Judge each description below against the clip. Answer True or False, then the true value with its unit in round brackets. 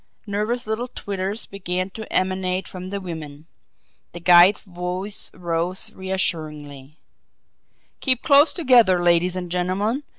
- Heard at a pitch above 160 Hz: True (185 Hz)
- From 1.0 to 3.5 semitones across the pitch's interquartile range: True (2.9 semitones)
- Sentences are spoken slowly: True (120 wpm)